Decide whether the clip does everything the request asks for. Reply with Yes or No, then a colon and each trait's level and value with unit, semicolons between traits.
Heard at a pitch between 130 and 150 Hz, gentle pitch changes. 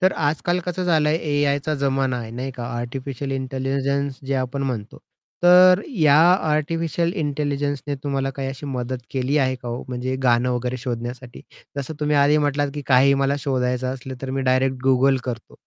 Yes: low, 135 Hz; narrow, 2.2 semitones